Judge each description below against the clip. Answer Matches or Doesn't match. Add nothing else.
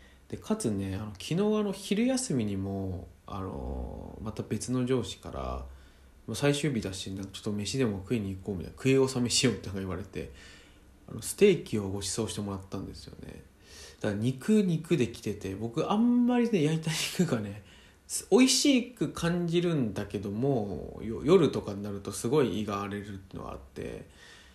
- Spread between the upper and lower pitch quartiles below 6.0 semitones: Doesn't match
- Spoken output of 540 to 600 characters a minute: Doesn't match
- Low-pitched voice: Matches